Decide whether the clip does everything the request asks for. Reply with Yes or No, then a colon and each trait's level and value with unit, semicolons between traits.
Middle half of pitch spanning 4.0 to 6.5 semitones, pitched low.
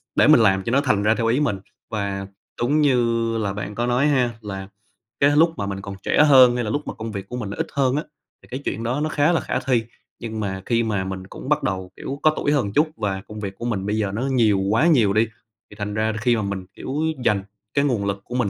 Yes: average, 4.9 semitones; low, 115 Hz